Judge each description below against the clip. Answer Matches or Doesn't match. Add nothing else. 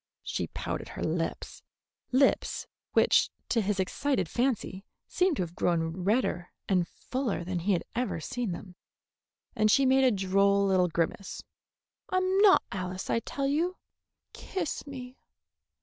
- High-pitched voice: Matches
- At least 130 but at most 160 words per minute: Matches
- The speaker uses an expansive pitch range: Matches